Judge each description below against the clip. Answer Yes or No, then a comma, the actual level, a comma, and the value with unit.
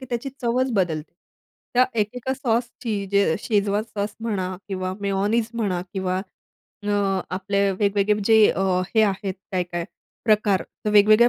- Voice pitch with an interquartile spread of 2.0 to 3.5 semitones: Yes, average, 2.7 semitones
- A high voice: Yes, high, 205 Hz